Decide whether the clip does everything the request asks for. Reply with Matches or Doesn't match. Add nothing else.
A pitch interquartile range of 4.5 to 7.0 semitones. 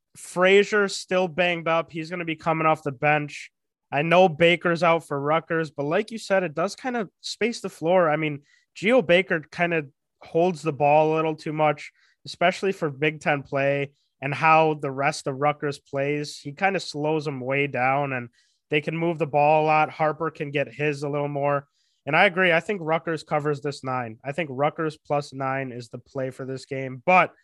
Doesn't match